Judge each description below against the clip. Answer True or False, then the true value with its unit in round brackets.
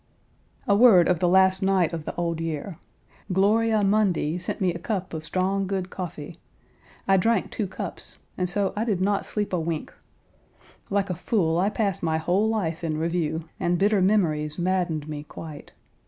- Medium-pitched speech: True (180 Hz)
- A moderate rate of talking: True (180 wpm)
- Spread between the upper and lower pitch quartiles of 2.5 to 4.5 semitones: True (3.3 semitones)